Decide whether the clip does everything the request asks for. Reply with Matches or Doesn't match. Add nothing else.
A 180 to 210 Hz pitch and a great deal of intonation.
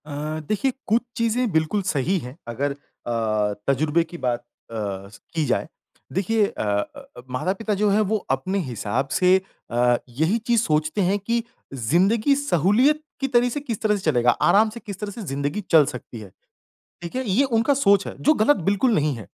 Matches